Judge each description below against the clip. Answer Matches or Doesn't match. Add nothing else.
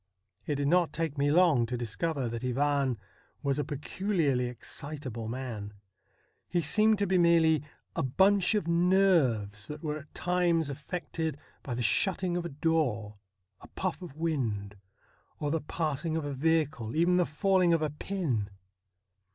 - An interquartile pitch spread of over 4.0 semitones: Matches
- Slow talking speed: Doesn't match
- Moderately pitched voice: Matches